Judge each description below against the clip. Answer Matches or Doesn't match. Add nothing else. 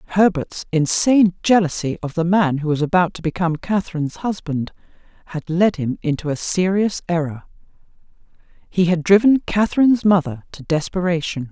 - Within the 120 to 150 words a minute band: Matches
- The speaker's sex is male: Doesn't match